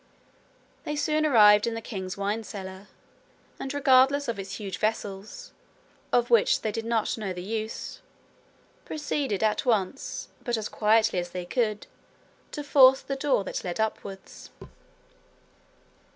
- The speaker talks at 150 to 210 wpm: No, average, 140 wpm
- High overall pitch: Yes, high, 220 Hz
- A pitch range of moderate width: Yes, average, 4.7 semitones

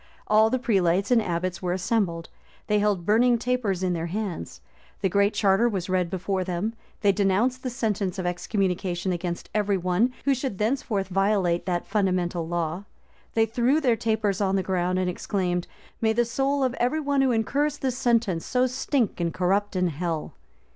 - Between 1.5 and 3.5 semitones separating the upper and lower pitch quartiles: No, average, 4.5 semitones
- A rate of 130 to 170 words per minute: No, average, 180 wpm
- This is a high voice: Yes, high, 200 Hz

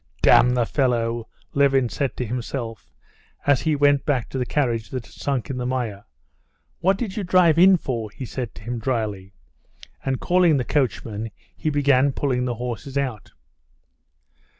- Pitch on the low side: Yes, low, 130 Hz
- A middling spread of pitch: Yes, average, 3.5 semitones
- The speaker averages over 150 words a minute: Yes, average, 170 wpm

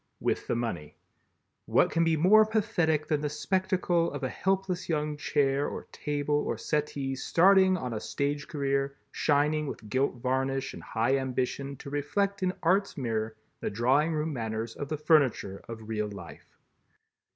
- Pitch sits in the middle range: Yes, medium, 145 Hz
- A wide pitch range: No, average, 4.1 semitones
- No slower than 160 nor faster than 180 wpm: Yes, average, 165 wpm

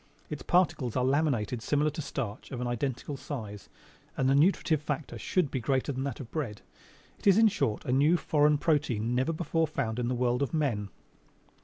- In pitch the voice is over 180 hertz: No, low, 135 Hz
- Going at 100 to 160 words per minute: No, average, 200 wpm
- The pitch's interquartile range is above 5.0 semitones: No, average, 3.8 semitones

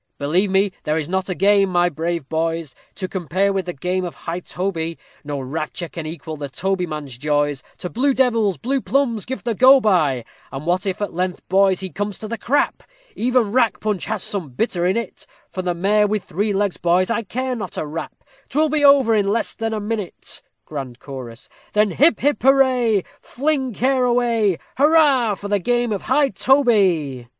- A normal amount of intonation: No, wide, 5.8 semitones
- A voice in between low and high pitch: No, high, 195 Hz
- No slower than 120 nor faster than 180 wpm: No, average, 195 wpm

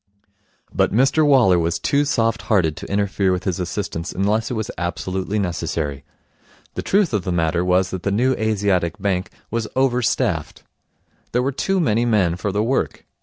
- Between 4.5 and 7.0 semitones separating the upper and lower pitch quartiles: Yes, average, 4.8 semitones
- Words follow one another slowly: No, average, 175 wpm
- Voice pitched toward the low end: Yes, low, 100 Hz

